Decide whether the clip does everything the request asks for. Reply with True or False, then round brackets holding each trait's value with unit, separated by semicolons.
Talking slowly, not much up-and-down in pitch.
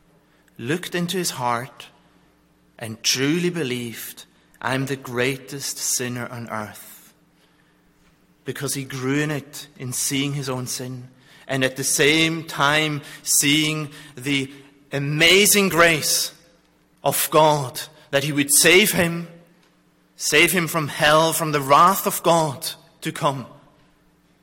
False (125 wpm; 3.7 semitones)